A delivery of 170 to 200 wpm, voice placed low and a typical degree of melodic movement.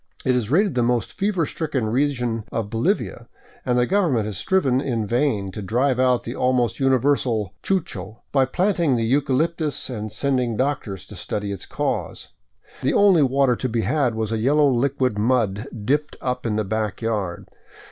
Yes: average, 175 wpm; low, 125 Hz; average, 4.2 semitones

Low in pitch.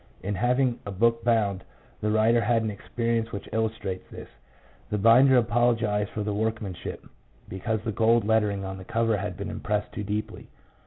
Yes: low, 110 Hz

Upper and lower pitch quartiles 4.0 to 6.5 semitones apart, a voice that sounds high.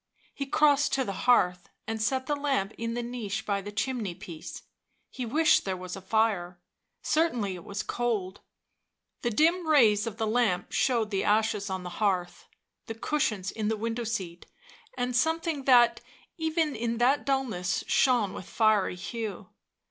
Yes: average, 4.7 semitones; high, 225 Hz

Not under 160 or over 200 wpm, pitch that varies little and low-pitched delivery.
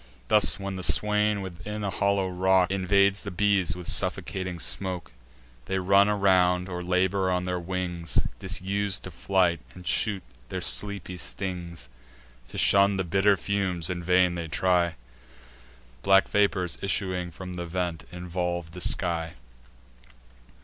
No: average, 140 wpm; narrow, 1.9 semitones; very low, 95 Hz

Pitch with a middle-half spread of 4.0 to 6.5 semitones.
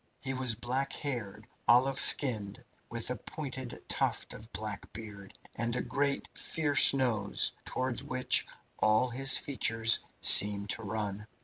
No: average, 3.5 semitones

